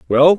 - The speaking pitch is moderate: Yes, medium, 160 Hz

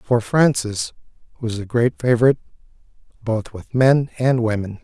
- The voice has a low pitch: Yes, low, 120 Hz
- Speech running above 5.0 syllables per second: No, 4.8 syllables/s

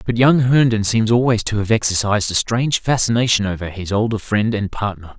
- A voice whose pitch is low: Yes, low, 110 Hz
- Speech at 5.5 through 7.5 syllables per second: Yes, 5.7 syllables/s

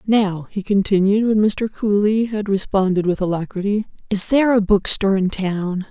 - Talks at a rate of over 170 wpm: No, average, 165 wpm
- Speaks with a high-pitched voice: Yes, high, 200 Hz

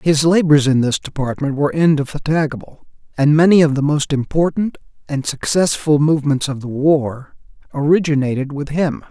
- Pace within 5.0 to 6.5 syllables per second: Yes, 5.2 syllables/s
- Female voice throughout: No, male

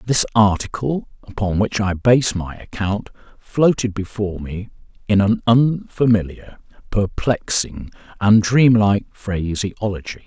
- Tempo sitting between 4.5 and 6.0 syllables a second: No, 4.0 syllables/s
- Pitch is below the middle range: Yes, low, 105 Hz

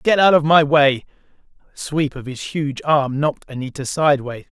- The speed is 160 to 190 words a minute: Yes, average, 185 wpm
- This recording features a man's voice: Yes, male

